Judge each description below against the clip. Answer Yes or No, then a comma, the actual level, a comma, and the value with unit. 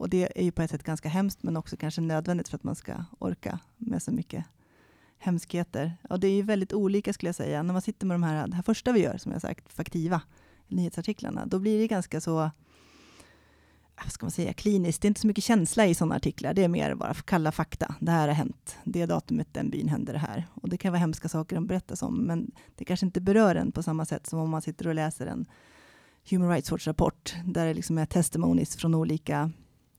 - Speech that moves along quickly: Yes, fast, 235 wpm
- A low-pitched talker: No, medium, 170 Hz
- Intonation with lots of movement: No, average, 3.1 semitones